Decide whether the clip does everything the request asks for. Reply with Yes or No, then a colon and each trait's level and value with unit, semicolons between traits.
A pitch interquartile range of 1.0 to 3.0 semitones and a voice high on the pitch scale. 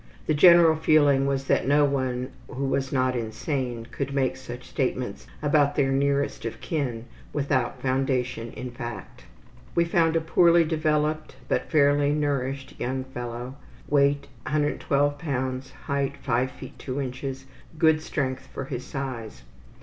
No: narrow, 2.4 semitones; low, 135 Hz